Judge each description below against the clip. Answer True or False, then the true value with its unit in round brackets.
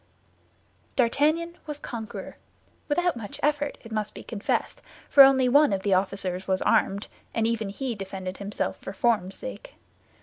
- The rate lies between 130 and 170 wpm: True (145 wpm)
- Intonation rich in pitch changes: True (6.6 semitones)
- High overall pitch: True (230 Hz)